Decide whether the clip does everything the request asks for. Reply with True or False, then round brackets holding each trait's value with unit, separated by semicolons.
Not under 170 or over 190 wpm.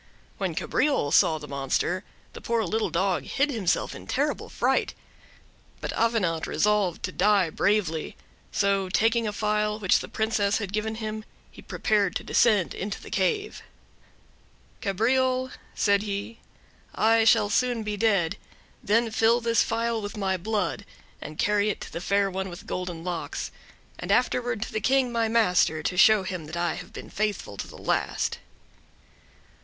False (160 wpm)